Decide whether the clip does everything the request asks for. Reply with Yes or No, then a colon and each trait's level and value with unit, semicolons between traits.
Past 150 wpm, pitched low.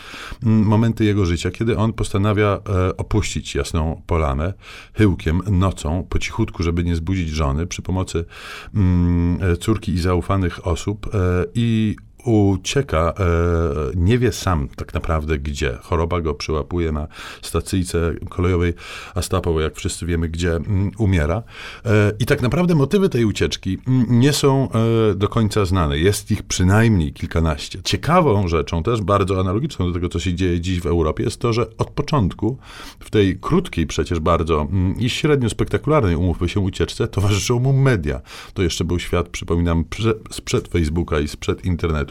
Yes: fast, 160 wpm; very low, 95 Hz